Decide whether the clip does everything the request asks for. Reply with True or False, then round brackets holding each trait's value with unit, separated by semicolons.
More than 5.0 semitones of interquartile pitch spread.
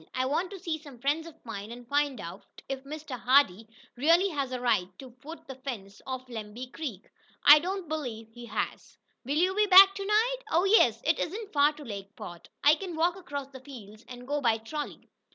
True (5.5 semitones)